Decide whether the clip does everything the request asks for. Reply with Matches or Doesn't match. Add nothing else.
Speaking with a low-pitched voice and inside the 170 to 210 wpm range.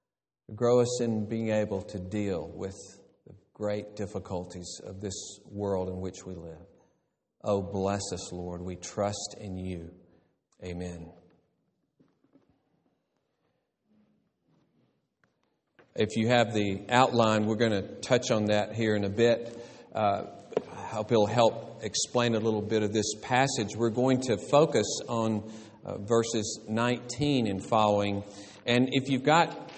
Doesn't match